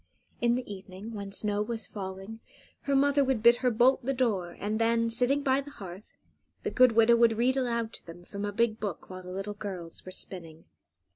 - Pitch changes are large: No, average, 3.9 semitones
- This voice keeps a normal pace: No, fast, 210 wpm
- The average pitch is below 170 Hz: No, high, 225 Hz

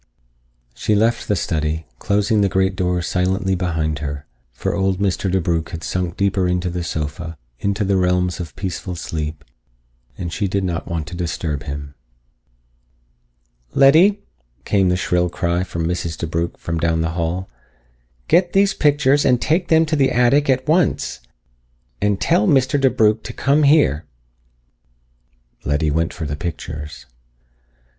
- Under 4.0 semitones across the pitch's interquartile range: No, average, 4.5 semitones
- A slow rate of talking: No, average, 150 wpm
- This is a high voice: No, very low, 90 Hz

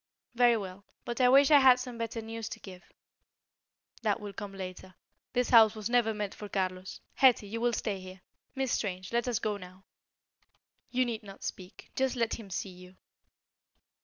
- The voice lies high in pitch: Yes, high, 215 Hz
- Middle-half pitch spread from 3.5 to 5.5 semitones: Yes, average, 3.9 semitones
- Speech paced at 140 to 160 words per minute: No, average, 185 wpm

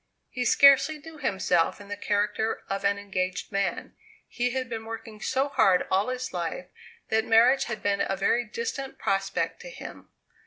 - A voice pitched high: Yes, high, 220 Hz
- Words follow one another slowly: No, average, 170 wpm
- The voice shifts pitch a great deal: No, average, 4.4 semitones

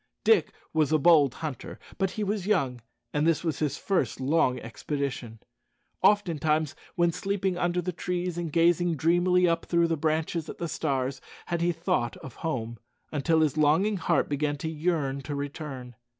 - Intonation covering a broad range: No, average, 3.6 semitones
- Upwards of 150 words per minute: Yes, average, 170 wpm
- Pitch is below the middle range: No, medium, 160 Hz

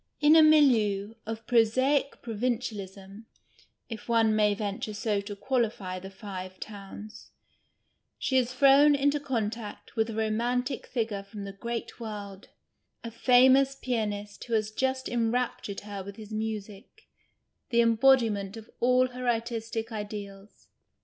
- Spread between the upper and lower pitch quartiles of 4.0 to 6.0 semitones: No, average, 3.3 semitones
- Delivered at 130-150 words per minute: Yes, slow, 135 wpm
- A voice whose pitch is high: Yes, high, 225 Hz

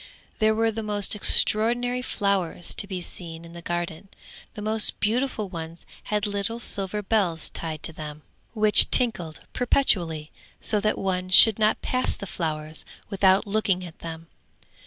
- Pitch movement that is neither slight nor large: Yes, average, 4.3 semitones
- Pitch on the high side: Yes, high, 195 Hz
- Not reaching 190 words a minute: Yes, average, 155 wpm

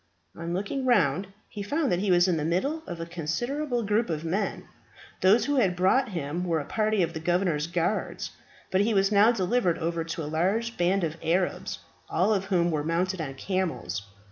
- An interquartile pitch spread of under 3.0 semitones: No, average, 4.0 semitones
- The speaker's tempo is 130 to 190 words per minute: No, average, 200 wpm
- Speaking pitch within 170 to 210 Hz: Yes, medium, 185 Hz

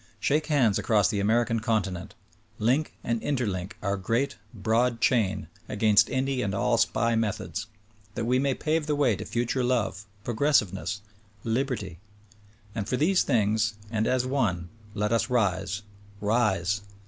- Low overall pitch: Yes, low, 115 Hz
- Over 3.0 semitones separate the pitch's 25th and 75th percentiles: Yes, average, 3.7 semitones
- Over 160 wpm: No, average, 150 wpm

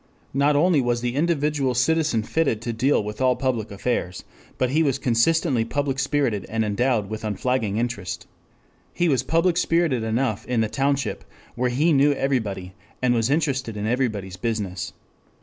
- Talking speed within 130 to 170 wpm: Yes, average, 165 wpm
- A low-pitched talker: Yes, low, 125 Hz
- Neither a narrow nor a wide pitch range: Yes, average, 4.3 semitones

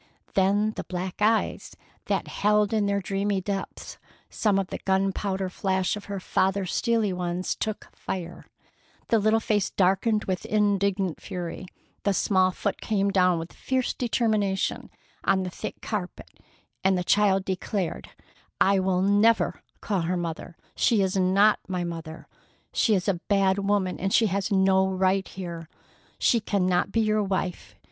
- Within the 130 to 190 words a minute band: Yes, average, 155 wpm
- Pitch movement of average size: No, narrow, 1.9 semitones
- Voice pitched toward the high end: Yes, high, 195 Hz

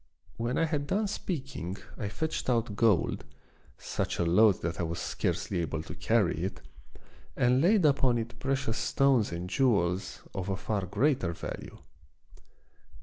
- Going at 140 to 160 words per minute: Yes, average, 150 wpm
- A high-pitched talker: No, low, 115 Hz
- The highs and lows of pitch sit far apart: Yes, wide, 6.9 semitones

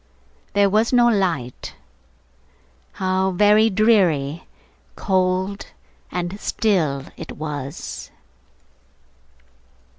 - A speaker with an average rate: No, slow, 70 wpm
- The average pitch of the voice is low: No, high, 190 Hz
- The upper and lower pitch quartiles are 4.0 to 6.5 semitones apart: Yes, average, 4.4 semitones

